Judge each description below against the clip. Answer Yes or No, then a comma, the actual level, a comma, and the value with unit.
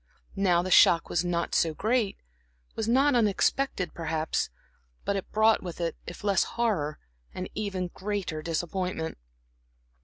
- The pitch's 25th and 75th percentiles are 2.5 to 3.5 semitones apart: No, average, 4.0 semitones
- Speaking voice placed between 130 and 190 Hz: Yes, medium, 185 Hz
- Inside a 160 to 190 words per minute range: No, average, 140 wpm